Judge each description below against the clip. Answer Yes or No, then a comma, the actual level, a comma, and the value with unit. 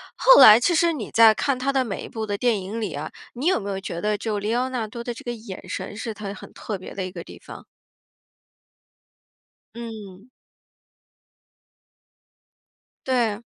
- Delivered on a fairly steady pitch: No, average, 3.2 semitones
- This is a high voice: Yes, high, 220 Hz